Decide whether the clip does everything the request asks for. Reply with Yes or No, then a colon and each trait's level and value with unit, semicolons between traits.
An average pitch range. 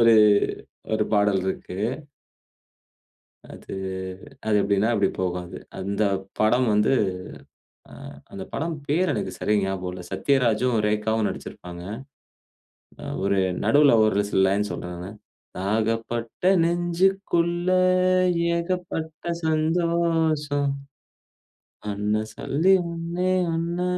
No: wide, 8.6 semitones